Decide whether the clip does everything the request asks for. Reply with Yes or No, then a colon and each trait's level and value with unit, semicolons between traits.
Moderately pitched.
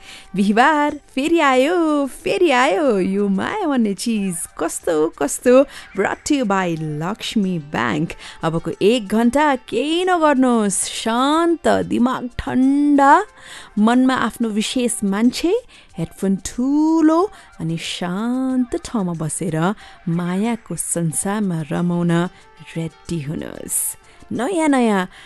No: high, 225 Hz